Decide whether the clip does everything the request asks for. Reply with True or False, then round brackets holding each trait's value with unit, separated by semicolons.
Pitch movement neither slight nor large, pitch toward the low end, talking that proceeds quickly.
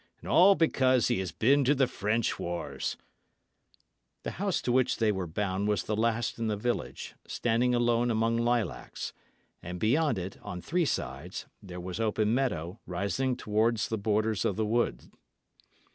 False (3.4 semitones; 110 Hz; 165 wpm)